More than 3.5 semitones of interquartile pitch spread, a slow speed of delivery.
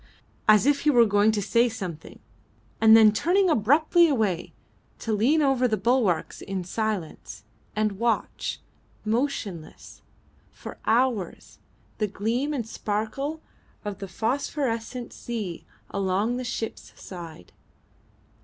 Yes: average, 3.9 semitones; slow, 120 wpm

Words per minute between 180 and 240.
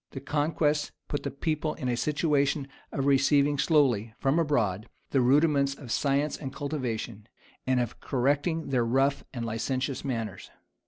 No: average, 155 wpm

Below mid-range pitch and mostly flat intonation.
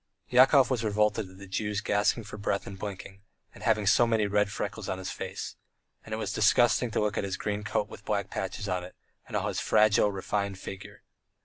Yes: low, 105 Hz; narrow, 1.7 semitones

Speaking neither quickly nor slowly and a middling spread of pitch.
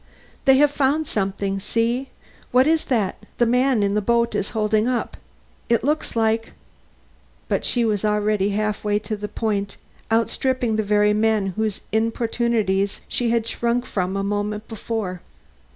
No: average, 160 wpm; narrow, 2.3 semitones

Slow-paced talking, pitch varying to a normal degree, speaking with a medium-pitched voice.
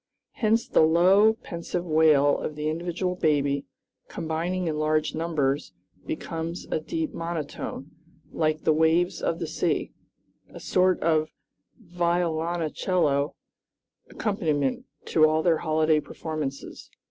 No: slow, 115 wpm; narrow, 2.3 semitones; medium, 160 Hz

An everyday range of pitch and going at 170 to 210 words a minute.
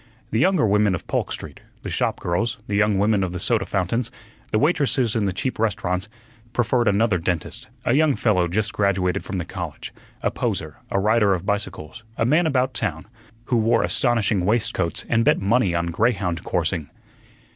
Yes: average, 4.2 semitones; average, 180 wpm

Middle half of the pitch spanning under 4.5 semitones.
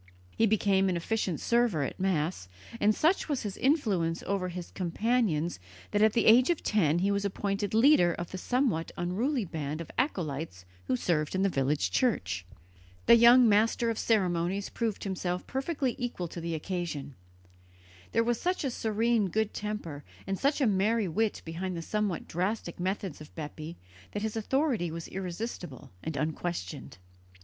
No: average, 5.2 semitones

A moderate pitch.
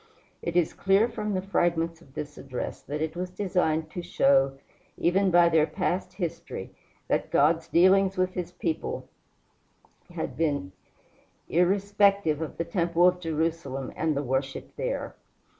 Yes: medium, 170 Hz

